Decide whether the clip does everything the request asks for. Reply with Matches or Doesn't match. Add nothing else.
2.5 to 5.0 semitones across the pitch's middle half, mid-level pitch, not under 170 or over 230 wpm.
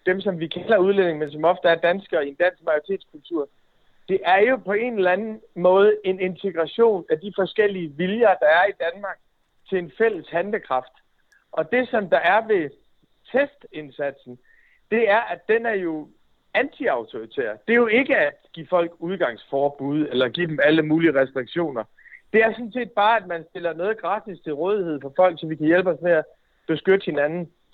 Doesn't match